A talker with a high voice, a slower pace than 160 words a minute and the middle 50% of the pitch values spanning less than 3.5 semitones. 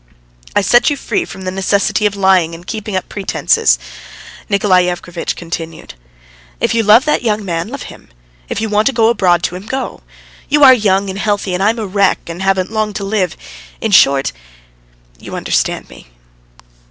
No: high, 200 Hz; average, 185 wpm; average, 3.0 semitones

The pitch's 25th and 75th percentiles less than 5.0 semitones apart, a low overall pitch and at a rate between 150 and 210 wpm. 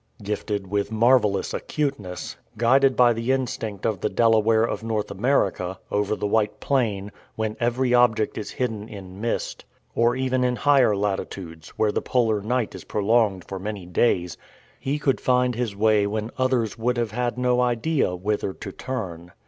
Yes: average, 3.4 semitones; low, 110 Hz; average, 165 wpm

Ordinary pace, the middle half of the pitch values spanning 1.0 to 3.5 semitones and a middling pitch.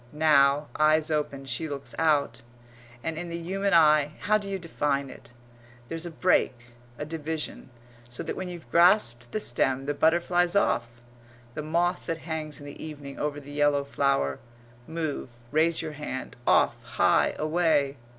Yes: average, 160 wpm; average, 3.0 semitones; medium, 155 Hz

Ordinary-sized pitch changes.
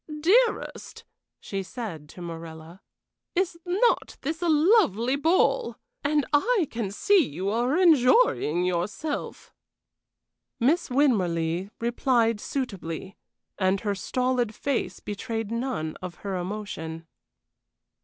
No: wide, 8.2 semitones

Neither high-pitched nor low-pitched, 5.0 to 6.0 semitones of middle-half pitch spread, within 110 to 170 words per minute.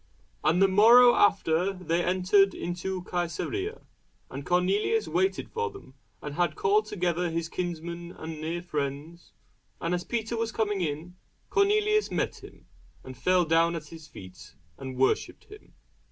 No: medium, 180 Hz; average, 4.2 semitones; average, 150 wpm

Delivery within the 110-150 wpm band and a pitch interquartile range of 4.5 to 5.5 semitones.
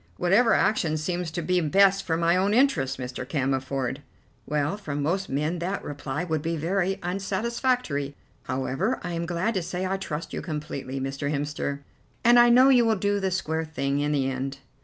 No: average, 185 wpm; average, 5.2 semitones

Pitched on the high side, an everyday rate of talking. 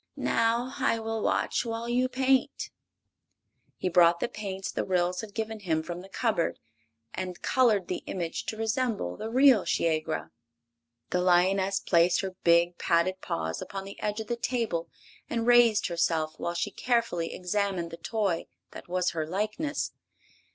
Yes: high, 195 Hz; average, 160 wpm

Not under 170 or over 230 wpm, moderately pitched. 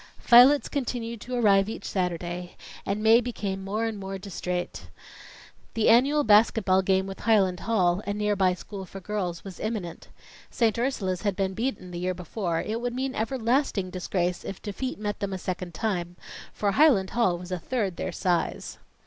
No: average, 180 wpm; high, 200 Hz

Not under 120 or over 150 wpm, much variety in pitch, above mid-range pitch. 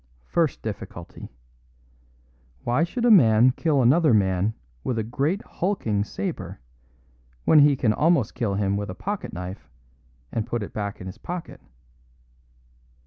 No: average, 140 wpm; wide, 7.5 semitones; low, 115 Hz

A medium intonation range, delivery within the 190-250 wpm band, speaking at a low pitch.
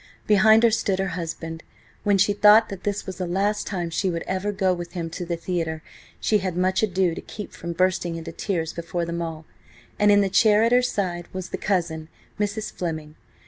No: average, 3.4 semitones; fast, 205 wpm; medium, 185 Hz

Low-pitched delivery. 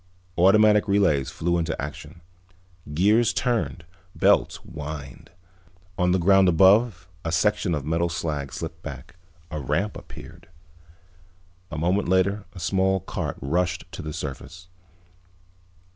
Yes: very low, 90 Hz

